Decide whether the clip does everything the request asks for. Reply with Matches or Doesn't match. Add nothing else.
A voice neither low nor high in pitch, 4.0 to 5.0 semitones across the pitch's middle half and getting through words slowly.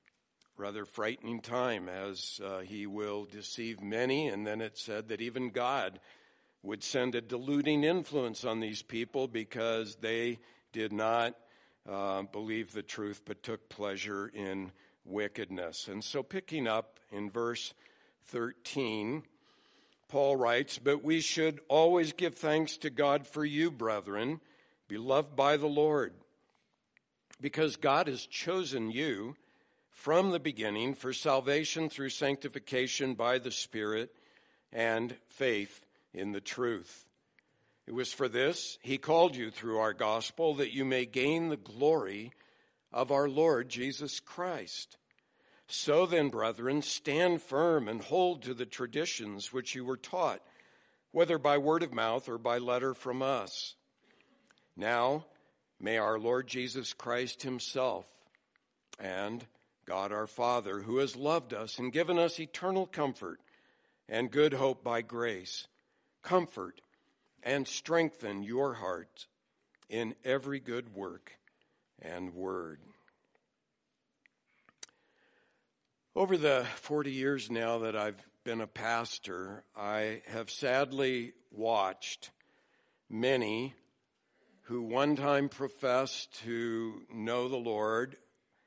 Doesn't match